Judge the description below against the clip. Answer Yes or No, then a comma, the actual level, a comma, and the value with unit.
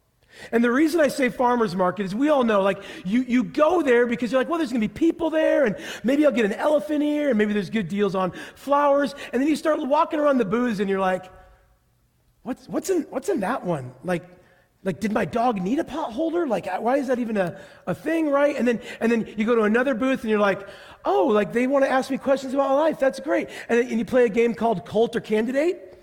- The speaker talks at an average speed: No, fast, 255 wpm